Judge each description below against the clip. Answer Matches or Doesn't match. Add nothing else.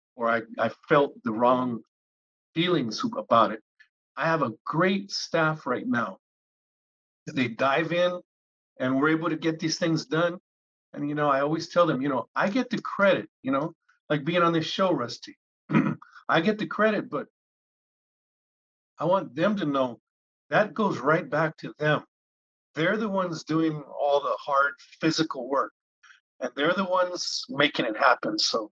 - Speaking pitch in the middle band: Matches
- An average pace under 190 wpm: Matches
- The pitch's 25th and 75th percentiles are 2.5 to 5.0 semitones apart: Matches